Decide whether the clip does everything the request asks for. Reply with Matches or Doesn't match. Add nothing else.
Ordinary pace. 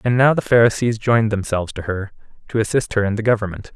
Doesn't match